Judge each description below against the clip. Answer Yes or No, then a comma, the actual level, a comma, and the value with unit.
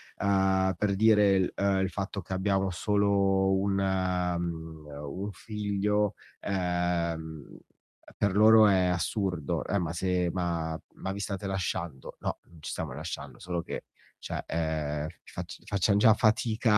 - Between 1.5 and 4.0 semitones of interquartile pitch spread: Yes, average, 2.7 semitones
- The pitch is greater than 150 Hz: No, very low, 95 Hz